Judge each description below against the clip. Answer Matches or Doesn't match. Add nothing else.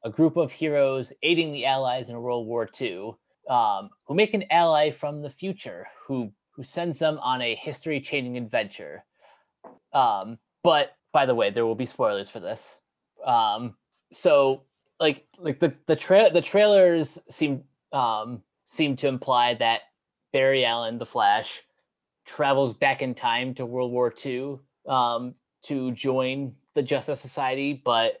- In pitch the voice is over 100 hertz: Matches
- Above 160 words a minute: Doesn't match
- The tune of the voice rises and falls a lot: Doesn't match